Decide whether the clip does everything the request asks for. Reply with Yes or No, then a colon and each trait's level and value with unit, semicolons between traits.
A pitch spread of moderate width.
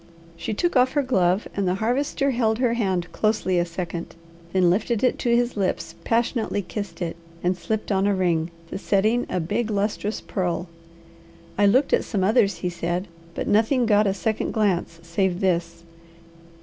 Yes: average, 4.0 semitones